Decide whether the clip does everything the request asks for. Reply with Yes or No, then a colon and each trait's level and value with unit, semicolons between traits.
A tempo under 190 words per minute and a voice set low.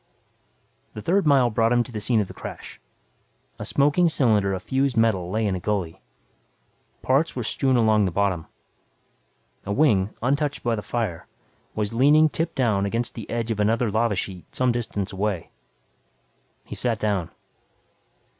Yes: average, 165 wpm; low, 115 Hz